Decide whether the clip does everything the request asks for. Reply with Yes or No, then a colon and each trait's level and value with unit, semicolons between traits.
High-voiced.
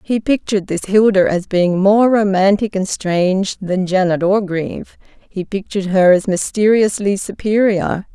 Yes: high, 195 Hz